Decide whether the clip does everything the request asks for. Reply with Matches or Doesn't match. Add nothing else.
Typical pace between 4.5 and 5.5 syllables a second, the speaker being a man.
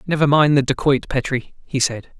Matches